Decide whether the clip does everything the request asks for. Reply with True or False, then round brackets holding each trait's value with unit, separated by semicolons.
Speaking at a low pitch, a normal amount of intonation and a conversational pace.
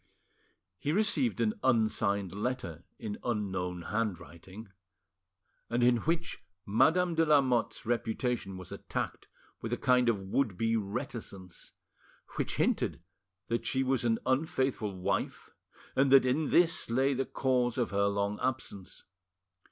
False (120 Hz; 4.6 semitones; 130 wpm)